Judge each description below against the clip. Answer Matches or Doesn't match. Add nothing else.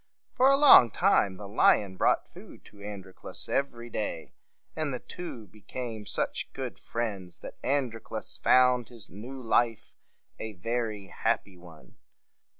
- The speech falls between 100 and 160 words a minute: Matches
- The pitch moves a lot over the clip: Doesn't match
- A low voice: Matches